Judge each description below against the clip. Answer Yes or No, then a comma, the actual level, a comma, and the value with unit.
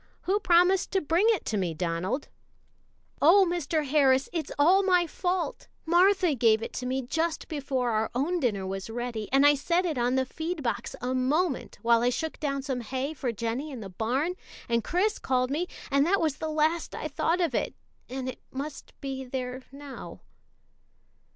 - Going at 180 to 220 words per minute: Yes, average, 190 wpm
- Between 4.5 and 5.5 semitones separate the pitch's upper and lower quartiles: Yes, average, 5.2 semitones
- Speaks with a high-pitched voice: Yes, very high, 275 Hz